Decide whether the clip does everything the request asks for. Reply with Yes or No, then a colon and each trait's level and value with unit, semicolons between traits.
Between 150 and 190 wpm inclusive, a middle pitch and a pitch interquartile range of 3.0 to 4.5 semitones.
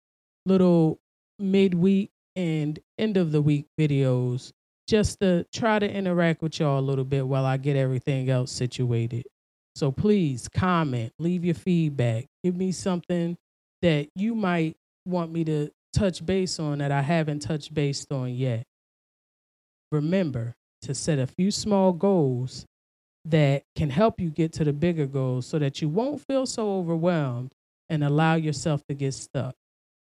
No: average, 155 wpm; medium, 155 Hz; average, 5.0 semitones